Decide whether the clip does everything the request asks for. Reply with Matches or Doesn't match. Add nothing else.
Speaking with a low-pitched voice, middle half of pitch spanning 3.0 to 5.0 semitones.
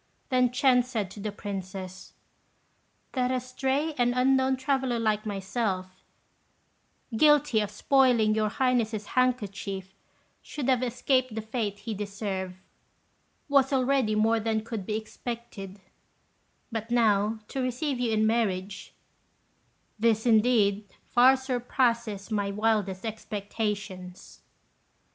Doesn't match